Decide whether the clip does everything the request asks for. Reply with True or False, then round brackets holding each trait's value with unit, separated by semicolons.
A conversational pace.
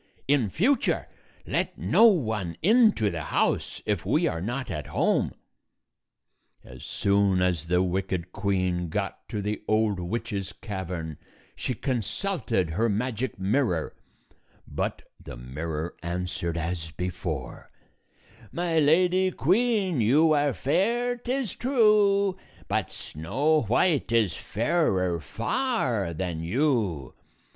False (120 wpm)